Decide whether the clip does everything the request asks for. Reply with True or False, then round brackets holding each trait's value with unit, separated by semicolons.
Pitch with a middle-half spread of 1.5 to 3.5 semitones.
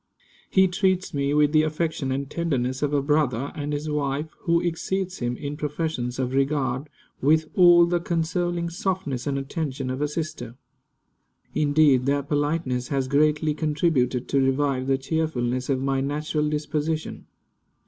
True (3.0 semitones)